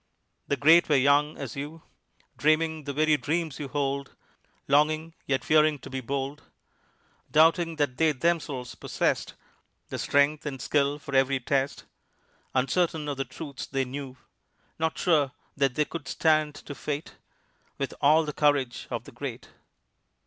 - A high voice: No, medium, 145 Hz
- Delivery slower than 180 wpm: Yes, average, 150 wpm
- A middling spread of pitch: No, narrow, 2.2 semitones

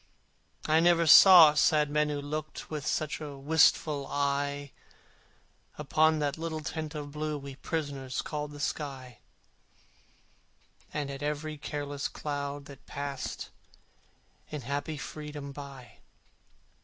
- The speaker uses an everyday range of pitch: No, narrow, 1.5 semitones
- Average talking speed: No, slow, 125 wpm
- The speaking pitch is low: No, medium, 145 Hz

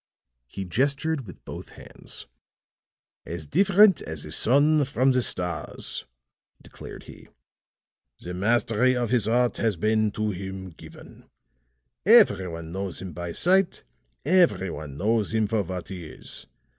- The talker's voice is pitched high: No, low, 110 Hz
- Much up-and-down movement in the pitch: Yes, wide, 6.4 semitones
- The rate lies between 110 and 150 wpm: Yes, average, 140 wpm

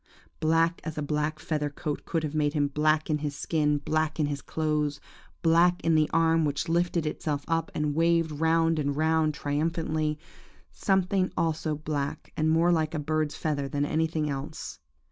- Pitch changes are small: Yes, narrow, 1.6 semitones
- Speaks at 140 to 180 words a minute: Yes, average, 175 wpm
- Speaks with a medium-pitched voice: Yes, medium, 155 Hz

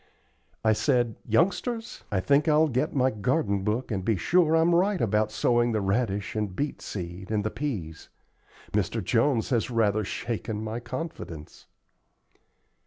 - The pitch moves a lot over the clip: Yes, wide, 5.8 semitones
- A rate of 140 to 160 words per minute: Yes, average, 150 wpm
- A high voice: No, low, 115 Hz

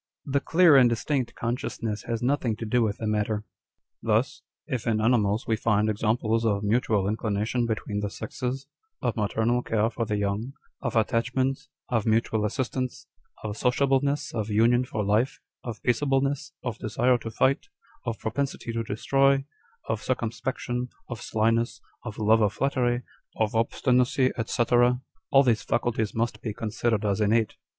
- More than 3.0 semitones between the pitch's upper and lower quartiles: No, average, 2.7 semitones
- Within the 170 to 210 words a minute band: No, average, 160 wpm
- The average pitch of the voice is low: Yes, low, 115 Hz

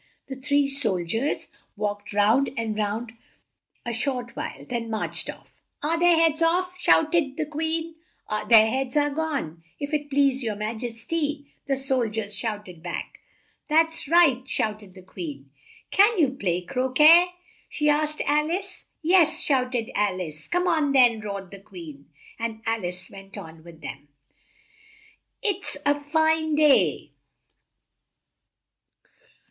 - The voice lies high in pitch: Yes, very high, 260 Hz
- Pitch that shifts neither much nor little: No, wide, 6.7 semitones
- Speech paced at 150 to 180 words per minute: Yes, average, 155 wpm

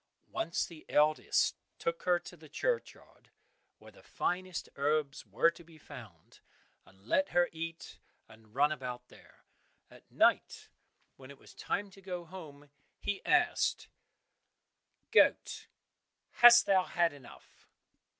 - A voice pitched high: No, medium, 160 Hz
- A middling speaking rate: No, slow, 130 wpm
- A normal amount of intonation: Yes, average, 4.6 semitones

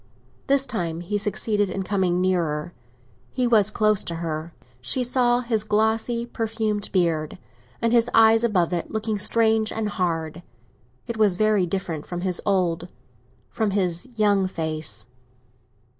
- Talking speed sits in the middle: No, slow, 130 wpm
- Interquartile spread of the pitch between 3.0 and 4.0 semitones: No, average, 4.6 semitones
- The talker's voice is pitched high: Yes, high, 195 Hz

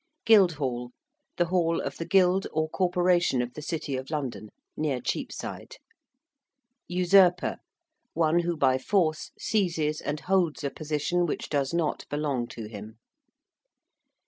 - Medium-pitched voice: Yes, medium, 155 Hz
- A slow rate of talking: Yes, slow, 130 wpm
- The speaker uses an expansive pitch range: No, average, 4.1 semitones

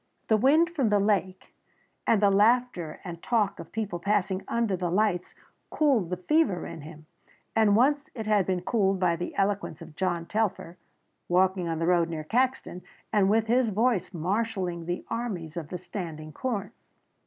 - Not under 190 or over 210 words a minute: No, average, 175 wpm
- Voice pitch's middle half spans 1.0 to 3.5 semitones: No, average, 4.2 semitones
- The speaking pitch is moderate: No, high, 195 Hz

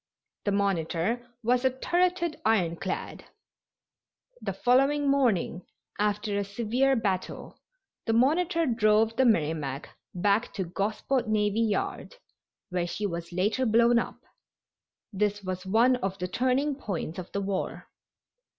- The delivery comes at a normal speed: No, slow, 125 wpm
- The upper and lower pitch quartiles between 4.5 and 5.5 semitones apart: Yes, average, 4.8 semitones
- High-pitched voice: Yes, high, 215 Hz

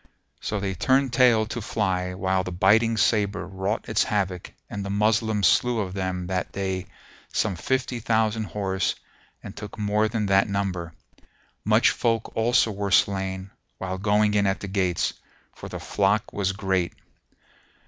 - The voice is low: Yes, low, 100 Hz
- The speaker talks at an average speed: Yes, average, 160 wpm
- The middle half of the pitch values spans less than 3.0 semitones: Yes, narrow, 2.4 semitones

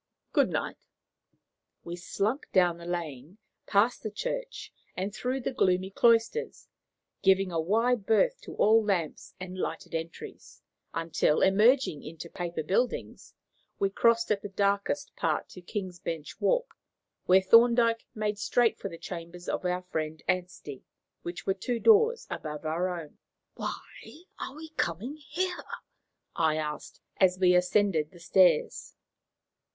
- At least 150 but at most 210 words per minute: No, average, 140 wpm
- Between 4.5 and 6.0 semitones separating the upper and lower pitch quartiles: Yes, average, 5.1 semitones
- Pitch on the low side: No, high, 190 Hz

